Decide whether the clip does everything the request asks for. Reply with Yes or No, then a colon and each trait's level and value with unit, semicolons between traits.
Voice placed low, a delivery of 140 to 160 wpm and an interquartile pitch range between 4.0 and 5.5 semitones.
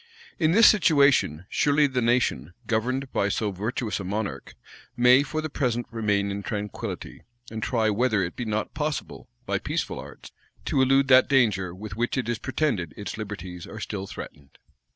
No: low, 115 Hz; average, 175 wpm; average, 4.6 semitones